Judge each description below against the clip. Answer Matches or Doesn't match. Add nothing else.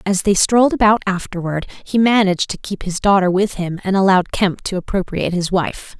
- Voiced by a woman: Matches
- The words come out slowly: Doesn't match